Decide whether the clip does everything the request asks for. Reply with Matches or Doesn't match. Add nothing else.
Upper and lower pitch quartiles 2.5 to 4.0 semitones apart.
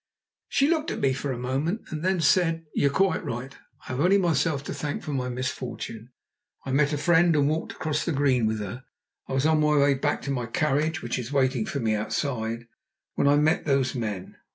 Matches